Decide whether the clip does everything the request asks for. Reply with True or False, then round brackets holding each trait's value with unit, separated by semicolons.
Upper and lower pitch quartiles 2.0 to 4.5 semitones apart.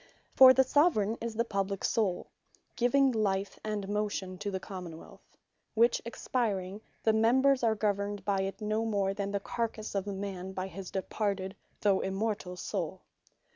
True (2.7 semitones)